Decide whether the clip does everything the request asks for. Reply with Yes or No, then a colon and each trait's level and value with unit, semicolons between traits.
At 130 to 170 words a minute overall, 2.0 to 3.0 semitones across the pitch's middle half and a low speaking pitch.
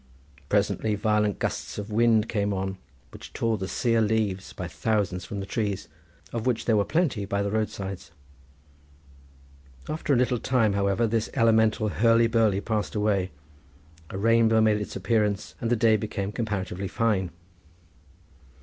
Yes: average, 150 wpm; narrow, 2.4 semitones; low, 105 Hz